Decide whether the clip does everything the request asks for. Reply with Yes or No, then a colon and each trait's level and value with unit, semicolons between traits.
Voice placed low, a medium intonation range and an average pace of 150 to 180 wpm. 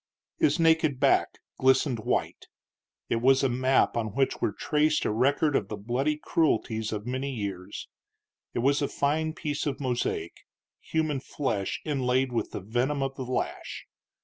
Yes: low, 130 Hz; average, 4.0 semitones; average, 160 wpm